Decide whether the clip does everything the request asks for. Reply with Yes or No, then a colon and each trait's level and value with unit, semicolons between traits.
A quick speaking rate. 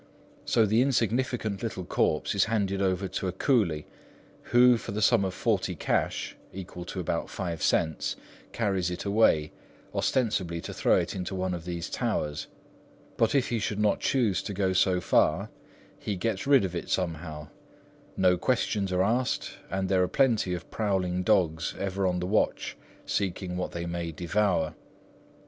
No: average, 165 wpm